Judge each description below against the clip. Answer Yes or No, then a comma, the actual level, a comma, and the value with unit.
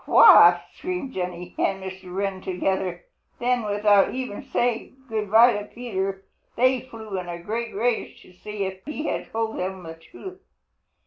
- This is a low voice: No, high, 205 Hz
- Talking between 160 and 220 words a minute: Yes, average, 165 wpm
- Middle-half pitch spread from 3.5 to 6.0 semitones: Yes, average, 4.1 semitones